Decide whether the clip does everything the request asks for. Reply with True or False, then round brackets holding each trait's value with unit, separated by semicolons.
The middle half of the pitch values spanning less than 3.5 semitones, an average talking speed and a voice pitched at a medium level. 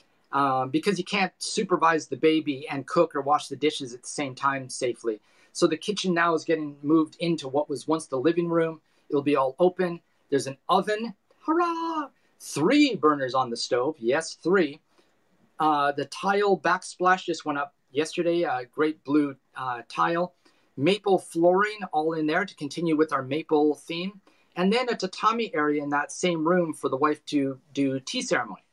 False (4.0 semitones; 180 wpm; 160 Hz)